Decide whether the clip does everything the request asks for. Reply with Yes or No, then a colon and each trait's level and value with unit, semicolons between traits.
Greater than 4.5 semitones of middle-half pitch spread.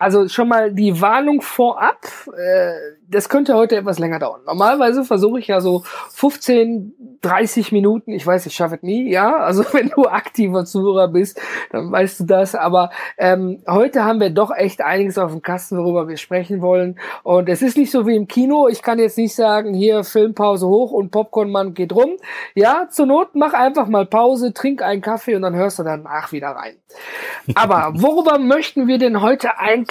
Yes: average, 5.2 semitones